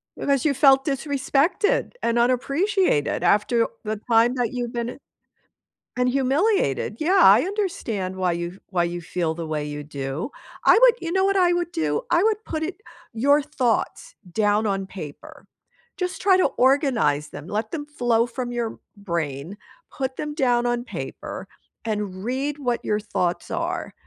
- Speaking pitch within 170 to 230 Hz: No, high, 240 Hz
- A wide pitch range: Yes, wide, 7.5 semitones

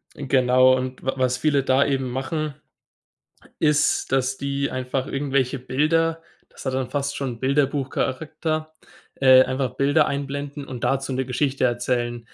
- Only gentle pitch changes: Yes, narrow, 1.8 semitones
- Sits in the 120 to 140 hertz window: Yes, low, 135 Hz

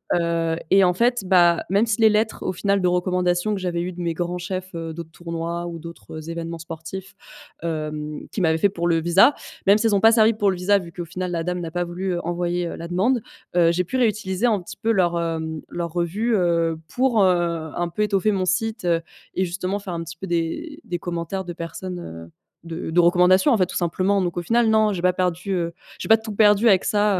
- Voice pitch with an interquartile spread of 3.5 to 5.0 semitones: No, average, 2.9 semitones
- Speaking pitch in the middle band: Yes, medium, 180 Hz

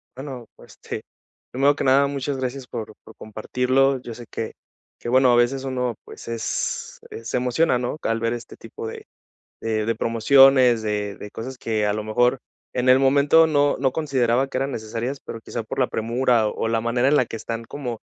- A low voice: Yes, low, 125 Hz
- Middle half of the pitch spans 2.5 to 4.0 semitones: Yes, average, 2.9 semitones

